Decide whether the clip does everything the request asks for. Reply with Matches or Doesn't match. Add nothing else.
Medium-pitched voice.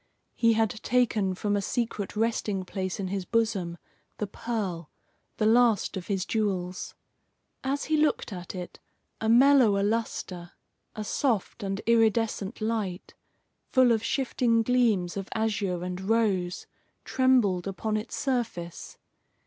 Doesn't match